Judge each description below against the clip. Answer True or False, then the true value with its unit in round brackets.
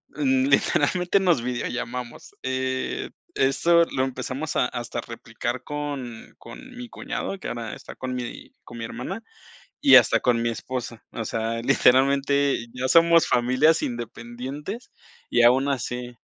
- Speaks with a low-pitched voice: True (130 Hz)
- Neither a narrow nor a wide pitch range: True (3.7 semitones)